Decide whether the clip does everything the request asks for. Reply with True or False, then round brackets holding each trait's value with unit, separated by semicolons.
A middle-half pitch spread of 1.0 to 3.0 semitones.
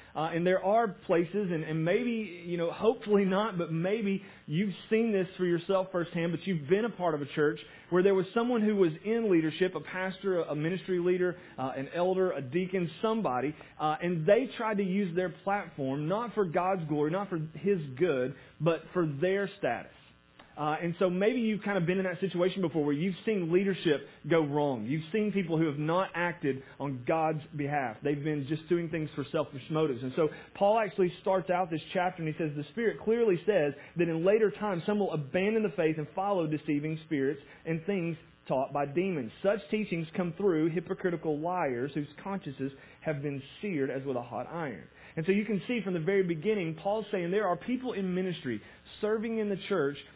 False (4.1 semitones)